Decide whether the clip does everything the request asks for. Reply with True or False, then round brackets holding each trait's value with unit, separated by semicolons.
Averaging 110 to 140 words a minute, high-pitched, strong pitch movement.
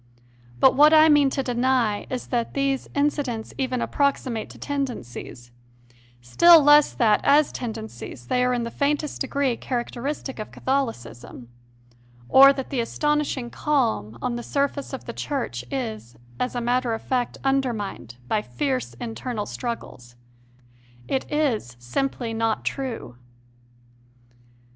False (135 wpm; 250 Hz; 3.8 semitones)